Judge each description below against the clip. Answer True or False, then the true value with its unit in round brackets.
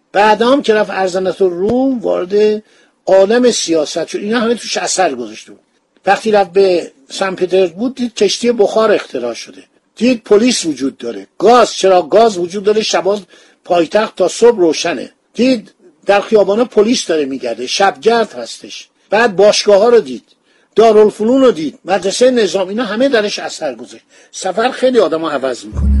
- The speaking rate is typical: False (160 wpm)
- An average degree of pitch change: True (4.0 semitones)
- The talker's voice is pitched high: True (210 Hz)